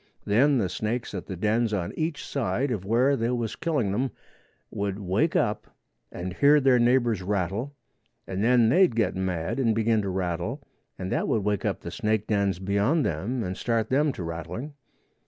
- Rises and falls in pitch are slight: No, average, 4.8 semitones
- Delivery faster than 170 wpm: Yes, average, 185 wpm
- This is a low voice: Yes, low, 110 Hz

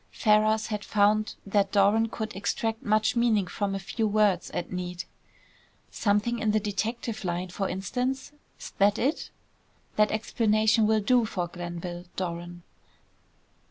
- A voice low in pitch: No, high, 210 Hz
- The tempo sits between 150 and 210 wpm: No, average, 140 wpm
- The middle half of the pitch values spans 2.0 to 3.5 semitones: Yes, narrow, 2.6 semitones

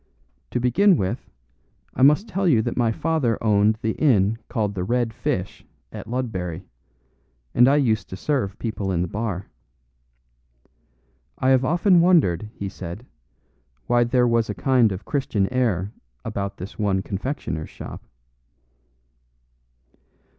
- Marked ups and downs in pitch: No, average, 4.9 semitones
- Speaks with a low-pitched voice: Yes, low, 115 Hz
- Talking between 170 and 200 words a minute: No, average, 140 wpm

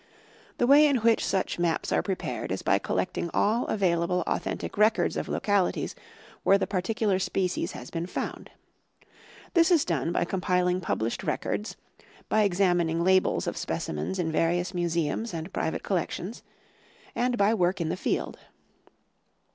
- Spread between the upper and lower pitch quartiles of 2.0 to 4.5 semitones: Yes, average, 3.5 semitones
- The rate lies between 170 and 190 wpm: No, average, 155 wpm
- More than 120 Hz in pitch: Yes, medium, 185 Hz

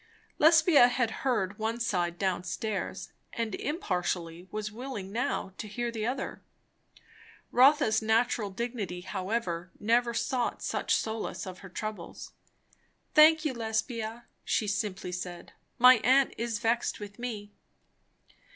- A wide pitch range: No, average, 4.0 semitones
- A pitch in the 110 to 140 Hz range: No, high, 220 Hz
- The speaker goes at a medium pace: No, slow, 125 wpm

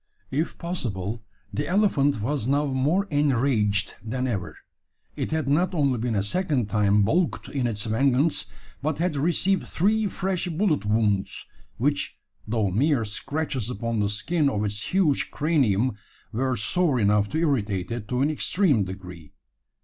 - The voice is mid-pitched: No, low, 130 Hz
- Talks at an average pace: Yes, average, 150 wpm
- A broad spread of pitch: Yes, wide, 6.8 semitones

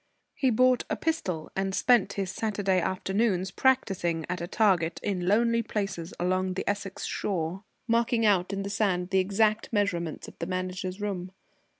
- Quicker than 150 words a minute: Yes, average, 165 wpm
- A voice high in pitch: Yes, high, 195 Hz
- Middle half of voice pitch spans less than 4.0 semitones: Yes, average, 2.9 semitones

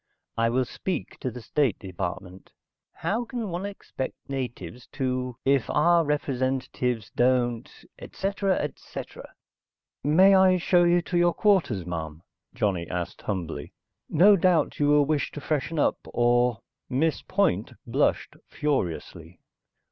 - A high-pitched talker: No, low, 135 Hz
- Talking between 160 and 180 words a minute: No, slow, 135 wpm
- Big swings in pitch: Yes, wide, 7.2 semitones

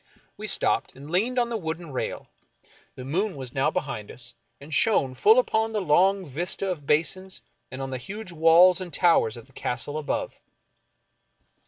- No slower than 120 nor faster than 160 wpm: No, average, 175 wpm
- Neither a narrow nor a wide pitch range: No, wide, 6.1 semitones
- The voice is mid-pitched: Yes, medium, 165 Hz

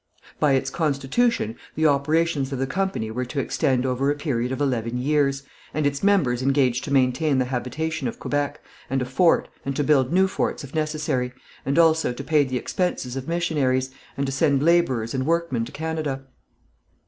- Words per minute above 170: Yes, average, 185 wpm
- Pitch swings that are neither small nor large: Yes, average, 3.5 semitones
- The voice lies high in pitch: No, medium, 140 Hz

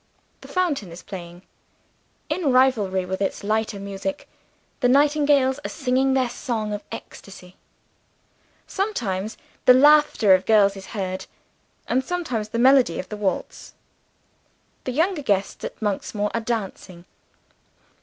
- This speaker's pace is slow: Yes, slow, 130 wpm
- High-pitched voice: Yes, high, 220 Hz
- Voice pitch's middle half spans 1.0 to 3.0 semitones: No, wide, 5.5 semitones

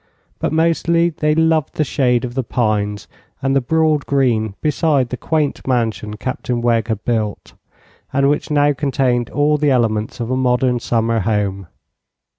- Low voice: Yes, low, 125 Hz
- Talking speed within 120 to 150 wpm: No, average, 160 wpm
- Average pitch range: Yes, average, 4.4 semitones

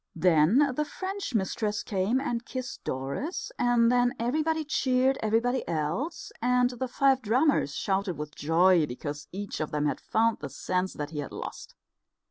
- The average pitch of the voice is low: No, high, 225 Hz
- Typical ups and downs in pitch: No, wide, 7.9 semitones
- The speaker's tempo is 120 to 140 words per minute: No, average, 160 wpm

